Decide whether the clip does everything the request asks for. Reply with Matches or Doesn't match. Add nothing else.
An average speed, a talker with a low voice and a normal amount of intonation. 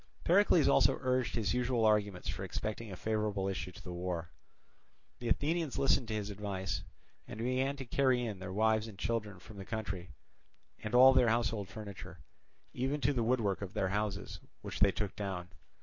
Matches